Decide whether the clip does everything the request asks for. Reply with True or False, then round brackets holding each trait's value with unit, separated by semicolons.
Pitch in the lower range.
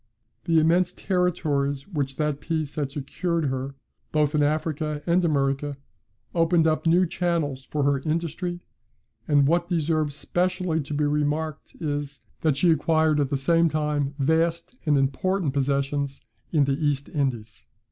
False (150 Hz)